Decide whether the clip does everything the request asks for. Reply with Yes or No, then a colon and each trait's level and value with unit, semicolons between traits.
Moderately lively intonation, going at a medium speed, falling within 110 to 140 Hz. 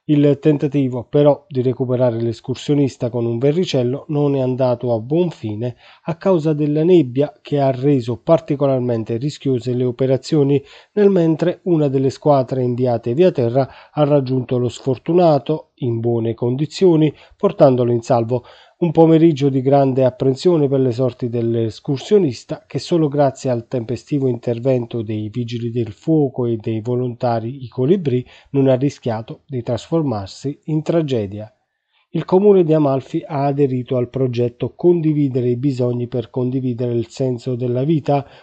Yes: average, 3.5 semitones; average, 145 wpm; low, 135 Hz